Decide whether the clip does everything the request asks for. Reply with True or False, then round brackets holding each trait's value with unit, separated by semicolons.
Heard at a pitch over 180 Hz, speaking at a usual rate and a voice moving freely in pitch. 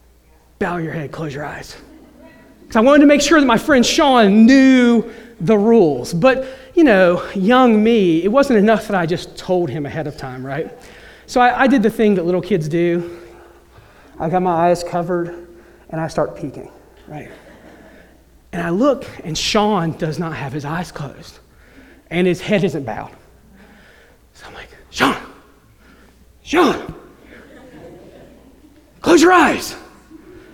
True (190 Hz; 155 wpm; 8.0 semitones)